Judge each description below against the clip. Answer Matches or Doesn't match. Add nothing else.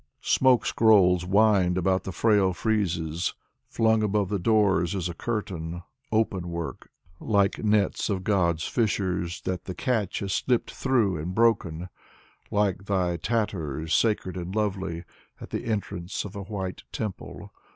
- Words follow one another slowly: Doesn't match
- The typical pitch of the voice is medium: Doesn't match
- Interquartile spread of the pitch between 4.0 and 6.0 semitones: Doesn't match